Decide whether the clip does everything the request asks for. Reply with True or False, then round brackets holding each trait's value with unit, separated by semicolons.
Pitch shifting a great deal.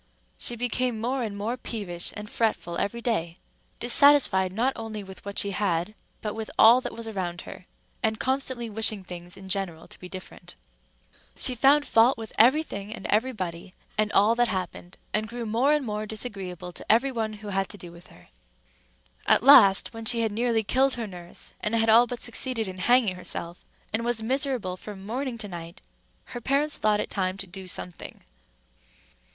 False (4.0 semitones)